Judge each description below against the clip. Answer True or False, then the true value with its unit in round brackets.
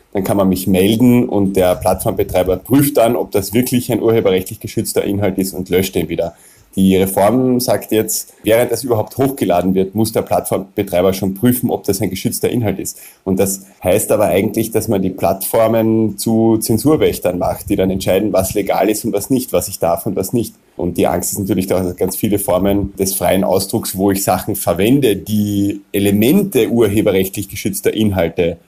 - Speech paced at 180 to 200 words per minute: True (190 wpm)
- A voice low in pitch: True (100 Hz)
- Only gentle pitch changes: False (3.0 semitones)